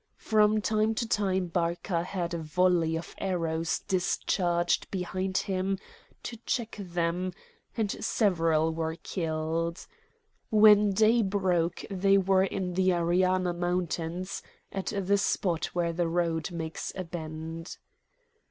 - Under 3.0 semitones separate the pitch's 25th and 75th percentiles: Yes, narrow, 2.6 semitones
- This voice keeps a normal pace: No, slow, 125 wpm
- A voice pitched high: No, medium, 180 Hz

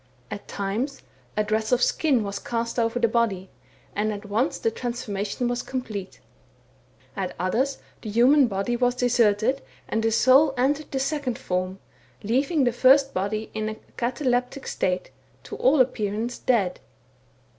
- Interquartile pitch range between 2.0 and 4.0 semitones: Yes, average, 3.6 semitones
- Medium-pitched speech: No, high, 235 Hz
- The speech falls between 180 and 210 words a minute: No, average, 150 wpm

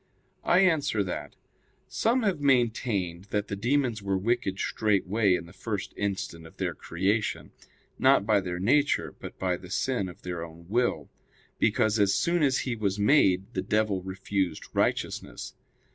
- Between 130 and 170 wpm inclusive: Yes, average, 160 wpm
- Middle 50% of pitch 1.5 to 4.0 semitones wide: No, average, 4.5 semitones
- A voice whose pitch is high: No, low, 100 Hz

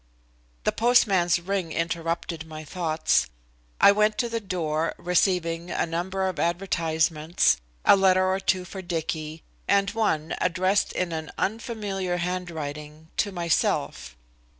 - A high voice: No, medium, 175 Hz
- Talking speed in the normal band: No, slow, 125 wpm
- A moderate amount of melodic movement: Yes, average, 3.0 semitones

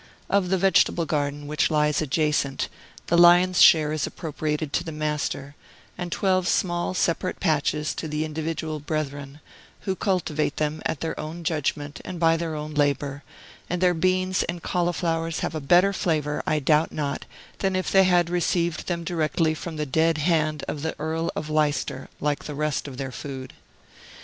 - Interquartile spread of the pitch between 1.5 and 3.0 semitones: Yes, narrow, 2.5 semitones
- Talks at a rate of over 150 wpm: Yes, average, 175 wpm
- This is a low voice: No, medium, 155 Hz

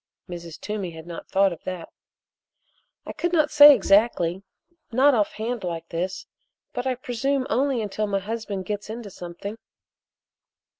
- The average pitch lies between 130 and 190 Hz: No, high, 210 Hz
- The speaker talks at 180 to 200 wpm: No, average, 150 wpm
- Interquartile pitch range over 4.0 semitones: Yes, average, 5.3 semitones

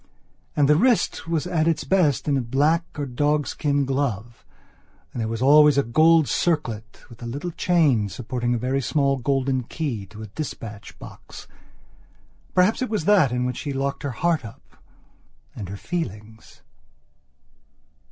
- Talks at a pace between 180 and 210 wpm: No, average, 165 wpm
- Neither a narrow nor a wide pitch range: Yes, average, 4.8 semitones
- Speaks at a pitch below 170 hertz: Yes, medium, 140 Hz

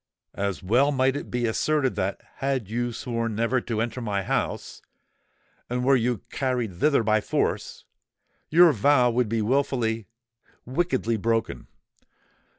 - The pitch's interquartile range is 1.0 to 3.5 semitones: Yes, average, 2.8 semitones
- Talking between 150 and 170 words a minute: No, slow, 135 wpm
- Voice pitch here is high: No, low, 120 Hz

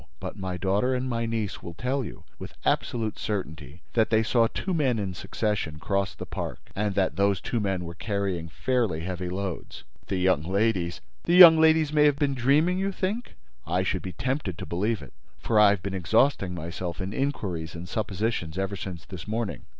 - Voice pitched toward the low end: Yes, low, 100 Hz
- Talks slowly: No, average, 195 wpm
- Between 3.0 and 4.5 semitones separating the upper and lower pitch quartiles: No, average, 5.2 semitones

